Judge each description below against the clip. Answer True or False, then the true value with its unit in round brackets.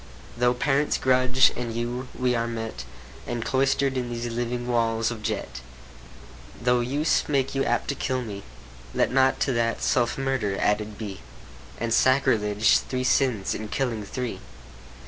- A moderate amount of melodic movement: False (2.3 semitones)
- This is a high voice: False (120 Hz)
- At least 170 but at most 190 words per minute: False (150 wpm)